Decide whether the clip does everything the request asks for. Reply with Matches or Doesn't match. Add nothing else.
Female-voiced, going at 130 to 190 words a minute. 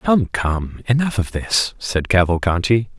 Doesn't match